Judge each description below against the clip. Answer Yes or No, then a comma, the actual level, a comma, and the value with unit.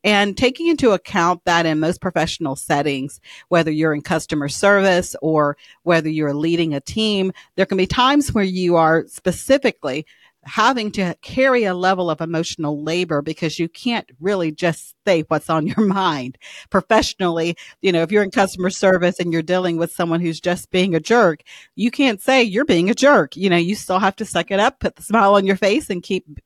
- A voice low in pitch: No, medium, 180 Hz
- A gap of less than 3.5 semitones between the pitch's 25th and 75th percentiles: No, average, 3.8 semitones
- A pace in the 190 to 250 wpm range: Yes, average, 200 wpm